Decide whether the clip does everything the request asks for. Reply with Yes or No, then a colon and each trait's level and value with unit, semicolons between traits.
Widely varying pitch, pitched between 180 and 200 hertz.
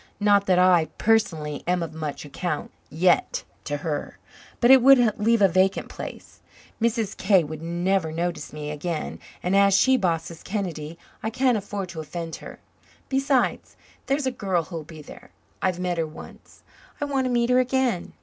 Yes: wide, 5.7 semitones; medium, 185 Hz